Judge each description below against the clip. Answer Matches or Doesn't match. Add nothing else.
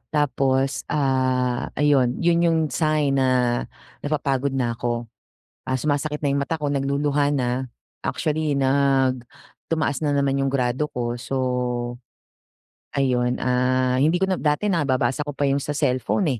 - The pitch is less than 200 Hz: Matches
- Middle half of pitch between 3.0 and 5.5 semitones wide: Doesn't match